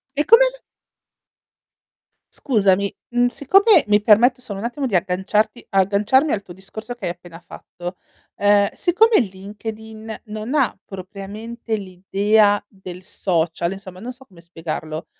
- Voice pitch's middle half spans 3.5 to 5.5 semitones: Yes, average, 3.9 semitones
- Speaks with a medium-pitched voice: No, high, 205 Hz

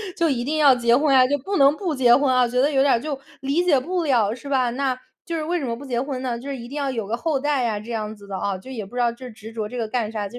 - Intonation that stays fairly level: No, average, 3.3 semitones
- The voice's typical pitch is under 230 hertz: No, very high, 255 Hz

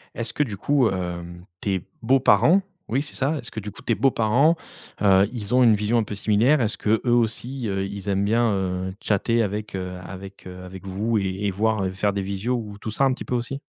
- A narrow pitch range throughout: No, average, 3.6 semitones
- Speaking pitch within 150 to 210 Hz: No, low, 105 Hz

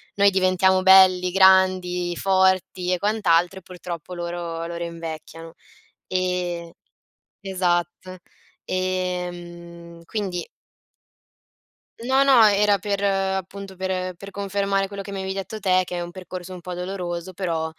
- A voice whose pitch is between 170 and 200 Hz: Yes, medium, 185 Hz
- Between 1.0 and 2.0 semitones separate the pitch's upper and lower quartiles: Yes, narrow, 1.7 semitones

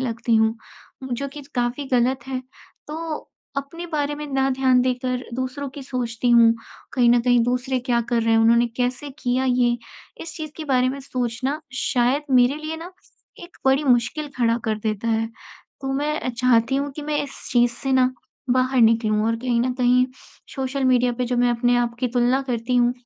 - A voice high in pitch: Yes, very high, 250 Hz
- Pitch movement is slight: Yes, narrow, 2.1 semitones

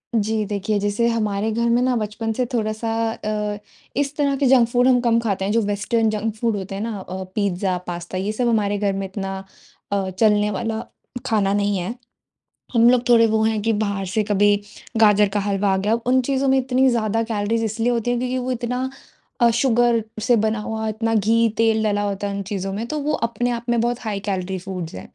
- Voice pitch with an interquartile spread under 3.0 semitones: Yes, narrow, 2.6 semitones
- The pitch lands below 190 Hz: No, high, 220 Hz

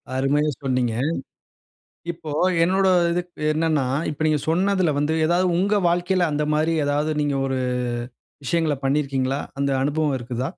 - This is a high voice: No, medium, 150 Hz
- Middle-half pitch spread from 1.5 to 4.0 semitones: Yes, average, 3.7 semitones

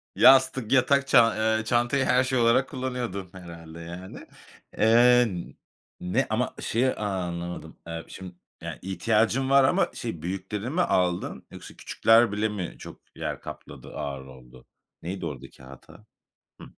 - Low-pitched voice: Yes, low, 105 Hz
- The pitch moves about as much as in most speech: No, wide, 6.1 semitones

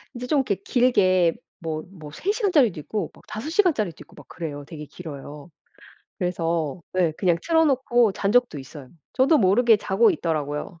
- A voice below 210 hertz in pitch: Yes, medium, 185 Hz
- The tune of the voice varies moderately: No, wide, 7.4 semitones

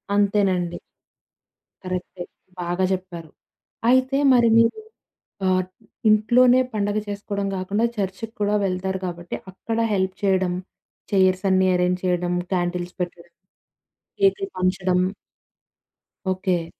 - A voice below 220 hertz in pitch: Yes, medium, 185 Hz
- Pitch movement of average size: No, narrow, 2.3 semitones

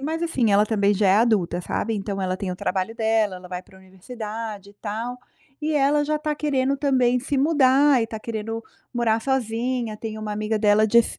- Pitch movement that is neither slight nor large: Yes, average, 4.0 semitones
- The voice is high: Yes, high, 225 Hz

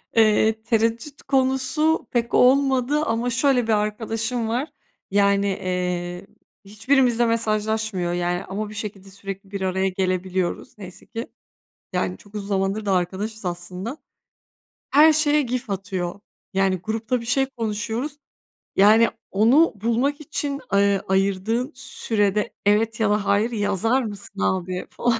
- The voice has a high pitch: Yes, high, 215 Hz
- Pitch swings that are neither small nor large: Yes, average, 3.8 semitones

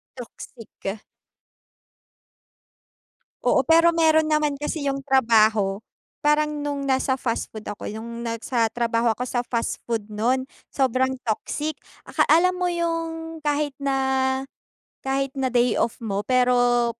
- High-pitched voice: Yes, very high, 260 Hz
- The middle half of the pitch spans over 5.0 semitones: No, average, 4.5 semitones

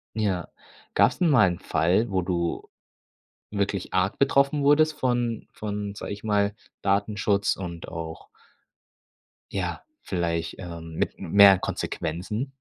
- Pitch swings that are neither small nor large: Yes, average, 3.9 semitones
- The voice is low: Yes, low, 100 Hz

